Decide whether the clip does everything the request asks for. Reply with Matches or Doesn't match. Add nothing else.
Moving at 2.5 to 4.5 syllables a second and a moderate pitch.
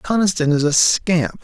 Matches